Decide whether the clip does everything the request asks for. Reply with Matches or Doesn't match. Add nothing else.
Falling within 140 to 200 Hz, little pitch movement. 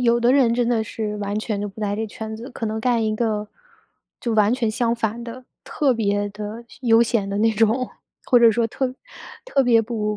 Doesn't match